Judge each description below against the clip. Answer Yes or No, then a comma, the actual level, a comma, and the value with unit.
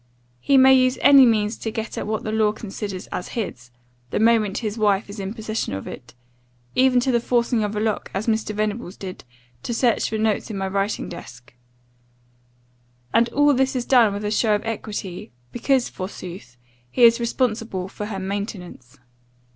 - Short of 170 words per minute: No, average, 185 wpm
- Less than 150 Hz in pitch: No, high, 215 Hz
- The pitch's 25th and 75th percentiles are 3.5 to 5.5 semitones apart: No, average, 3.1 semitones